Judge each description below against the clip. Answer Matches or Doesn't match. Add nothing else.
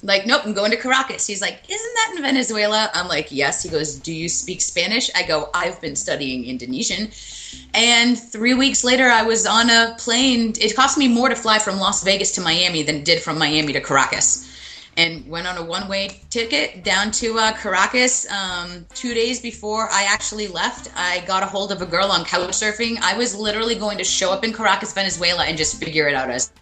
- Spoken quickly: Matches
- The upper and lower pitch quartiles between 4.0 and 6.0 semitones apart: Matches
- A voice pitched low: Doesn't match